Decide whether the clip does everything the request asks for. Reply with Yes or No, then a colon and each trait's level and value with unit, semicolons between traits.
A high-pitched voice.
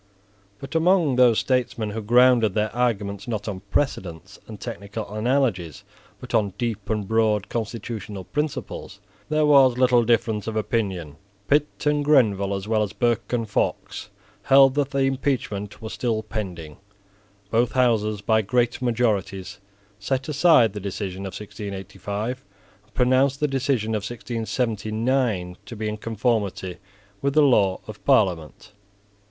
No: low, 110 Hz